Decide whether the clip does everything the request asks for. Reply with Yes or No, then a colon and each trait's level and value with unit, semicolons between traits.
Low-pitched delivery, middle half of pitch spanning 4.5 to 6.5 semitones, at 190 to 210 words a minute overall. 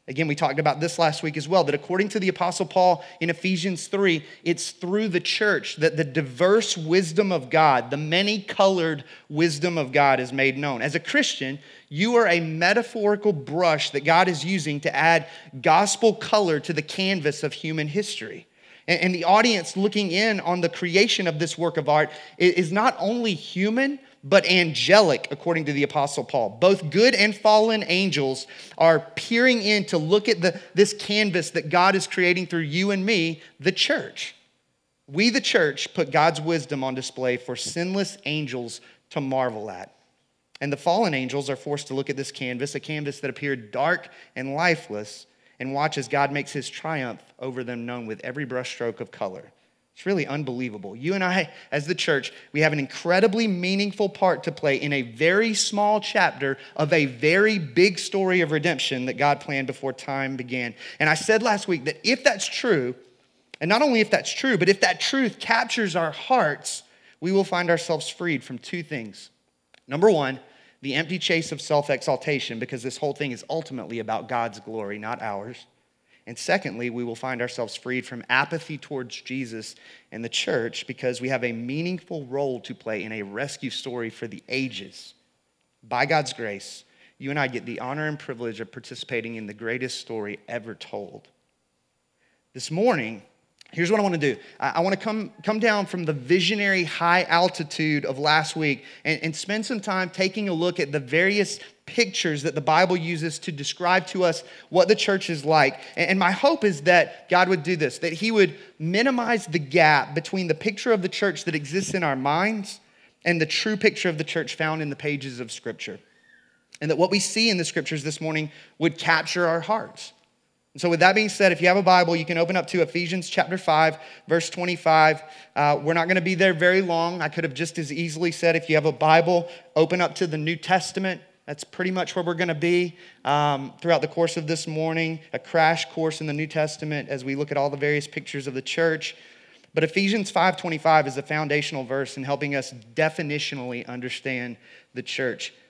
No: medium, 165 Hz; average, 4.8 semitones; average, 200 wpm